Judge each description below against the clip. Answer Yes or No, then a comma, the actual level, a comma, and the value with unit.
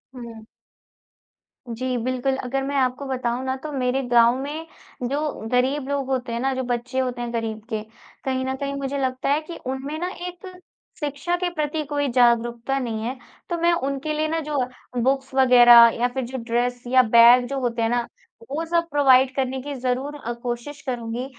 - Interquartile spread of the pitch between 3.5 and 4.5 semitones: No, average, 2.7 semitones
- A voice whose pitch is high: Yes, very high, 260 Hz